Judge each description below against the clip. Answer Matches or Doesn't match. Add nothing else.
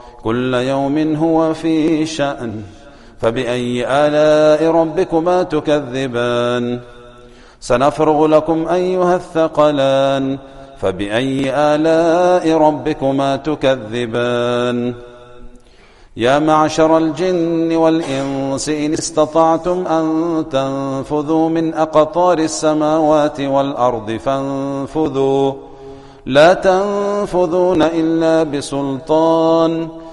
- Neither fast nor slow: Doesn't match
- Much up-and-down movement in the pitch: Doesn't match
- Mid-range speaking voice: Matches